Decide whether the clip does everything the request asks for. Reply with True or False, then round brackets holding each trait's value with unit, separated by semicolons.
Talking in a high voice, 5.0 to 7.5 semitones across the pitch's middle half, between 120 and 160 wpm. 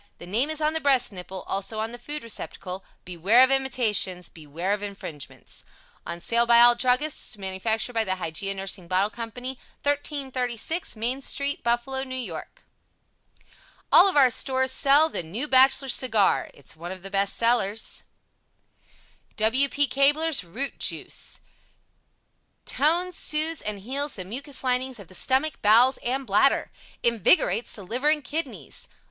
True (240 Hz; 5.6 semitones; 155 wpm)